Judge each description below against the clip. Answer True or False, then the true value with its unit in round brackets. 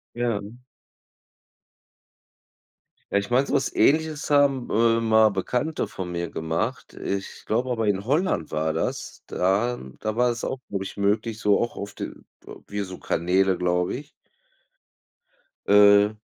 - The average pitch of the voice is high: False (110 Hz)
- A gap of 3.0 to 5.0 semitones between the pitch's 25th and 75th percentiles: True (4.2 semitones)